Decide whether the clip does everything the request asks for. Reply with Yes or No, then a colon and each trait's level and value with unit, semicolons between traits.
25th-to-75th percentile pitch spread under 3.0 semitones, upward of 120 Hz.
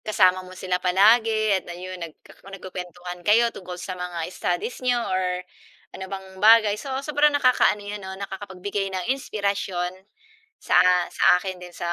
Yes: narrow, 2.6 semitones; high, 190 Hz